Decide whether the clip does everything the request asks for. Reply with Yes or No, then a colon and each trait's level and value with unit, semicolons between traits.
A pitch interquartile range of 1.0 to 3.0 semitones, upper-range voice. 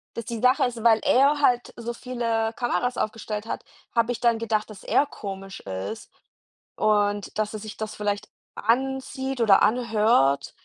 Yes: narrow, 2.6 semitones; high, 225 Hz